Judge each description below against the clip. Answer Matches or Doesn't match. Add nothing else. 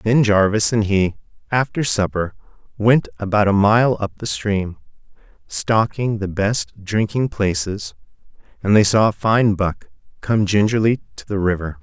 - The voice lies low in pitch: Matches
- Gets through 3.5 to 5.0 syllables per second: Matches